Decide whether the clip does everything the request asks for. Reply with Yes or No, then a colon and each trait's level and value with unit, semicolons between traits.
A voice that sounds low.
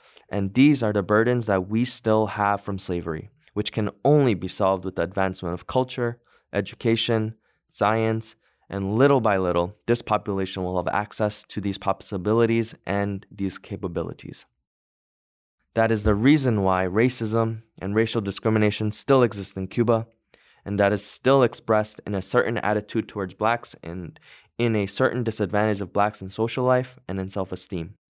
Yes: low, 105 Hz